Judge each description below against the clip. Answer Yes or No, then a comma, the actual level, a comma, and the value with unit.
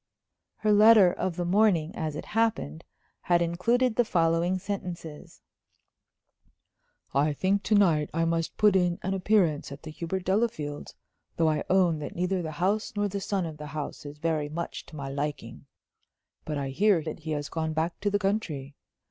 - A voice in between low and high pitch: Yes, medium, 170 Hz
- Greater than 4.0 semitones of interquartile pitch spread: Yes, average, 4.4 semitones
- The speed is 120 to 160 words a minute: No, average, 180 wpm